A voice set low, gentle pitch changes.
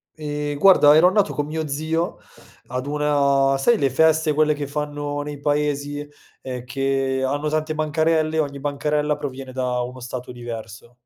No: medium, 145 Hz; narrow, 2.1 semitones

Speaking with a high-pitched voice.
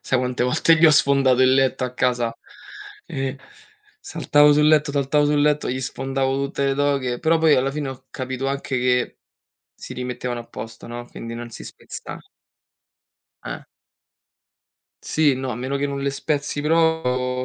No: low, 135 Hz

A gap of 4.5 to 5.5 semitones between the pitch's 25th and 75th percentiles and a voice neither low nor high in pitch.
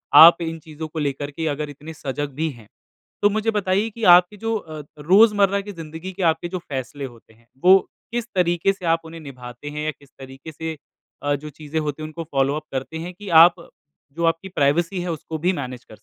No: average, 3.9 semitones; medium, 160 Hz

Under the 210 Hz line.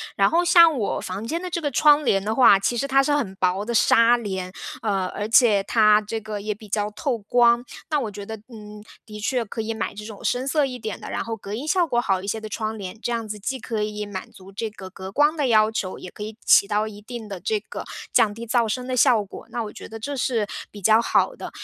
No: high, 220 Hz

